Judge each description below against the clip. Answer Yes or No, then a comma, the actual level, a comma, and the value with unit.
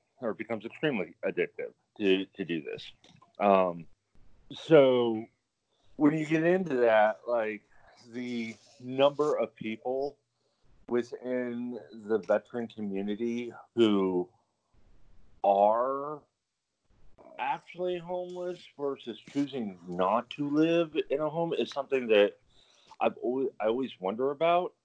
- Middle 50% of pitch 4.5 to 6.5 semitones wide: Yes, average, 5.3 semitones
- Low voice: Yes, low, 120 Hz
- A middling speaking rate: No, slow, 110 wpm